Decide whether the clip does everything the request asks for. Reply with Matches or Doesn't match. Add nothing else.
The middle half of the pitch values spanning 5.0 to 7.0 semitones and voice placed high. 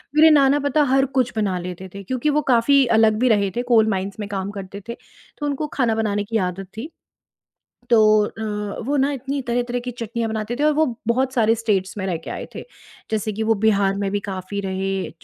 Doesn't match